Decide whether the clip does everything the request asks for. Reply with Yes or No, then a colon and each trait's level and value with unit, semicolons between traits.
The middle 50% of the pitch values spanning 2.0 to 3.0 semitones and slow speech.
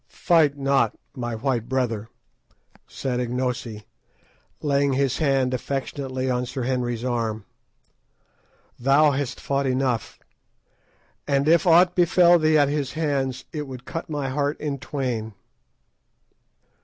Yes: narrow, 2.6 semitones; slow, 120 wpm